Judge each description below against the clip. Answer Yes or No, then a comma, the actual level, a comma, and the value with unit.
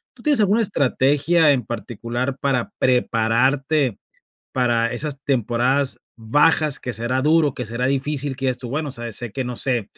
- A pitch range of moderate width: Yes, average, 3.2 semitones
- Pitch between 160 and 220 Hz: No, low, 130 Hz